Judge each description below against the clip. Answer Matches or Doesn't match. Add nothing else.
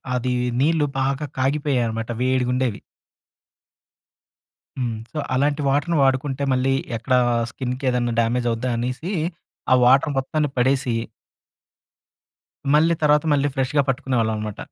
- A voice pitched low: Matches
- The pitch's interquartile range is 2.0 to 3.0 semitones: Matches